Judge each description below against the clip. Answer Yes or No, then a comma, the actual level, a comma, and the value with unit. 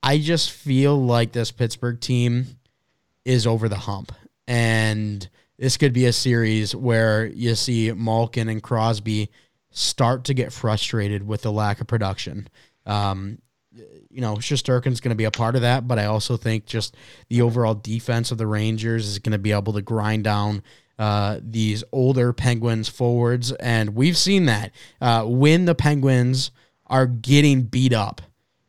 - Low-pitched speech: Yes, low, 115 Hz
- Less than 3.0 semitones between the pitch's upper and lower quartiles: Yes, narrow, 2.6 semitones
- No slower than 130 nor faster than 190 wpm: Yes, average, 165 wpm